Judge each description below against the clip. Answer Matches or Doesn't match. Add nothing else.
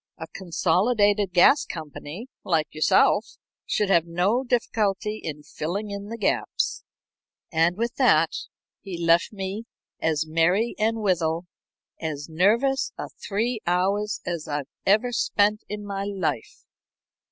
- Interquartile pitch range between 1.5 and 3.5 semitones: Doesn't match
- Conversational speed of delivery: Doesn't match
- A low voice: Doesn't match